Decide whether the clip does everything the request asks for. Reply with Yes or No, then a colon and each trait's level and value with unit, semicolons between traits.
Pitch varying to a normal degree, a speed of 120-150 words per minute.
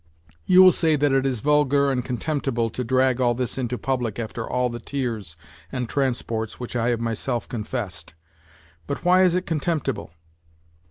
No: average, 3.2 semitones; average, 180 wpm